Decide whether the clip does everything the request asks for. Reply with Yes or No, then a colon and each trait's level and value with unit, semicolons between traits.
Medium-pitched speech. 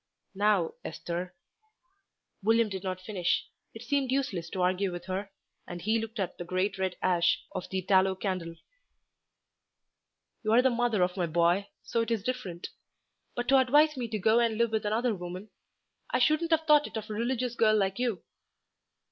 No: high, 210 Hz